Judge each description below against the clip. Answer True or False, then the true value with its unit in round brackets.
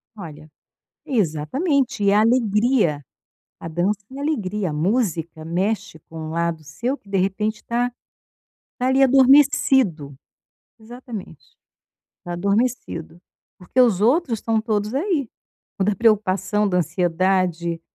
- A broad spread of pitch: True (5.9 semitones)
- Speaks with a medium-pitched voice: False (205 Hz)